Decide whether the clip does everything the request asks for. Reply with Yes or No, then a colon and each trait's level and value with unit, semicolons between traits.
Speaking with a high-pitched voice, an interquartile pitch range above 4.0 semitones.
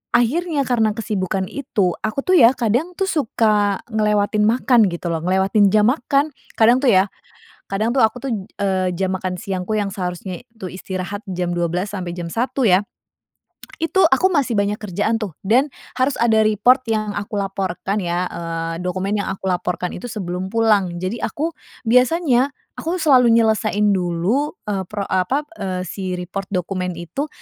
Yes: high, 205 Hz; average, 4.6 semitones